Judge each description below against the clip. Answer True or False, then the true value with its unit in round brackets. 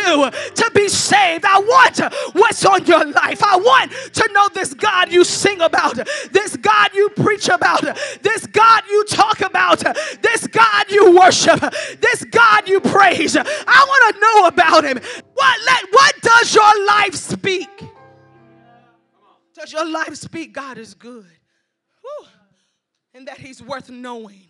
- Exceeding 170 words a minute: False (150 wpm)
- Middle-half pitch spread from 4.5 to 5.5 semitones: True (5.0 semitones)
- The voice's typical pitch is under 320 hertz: False (385 Hz)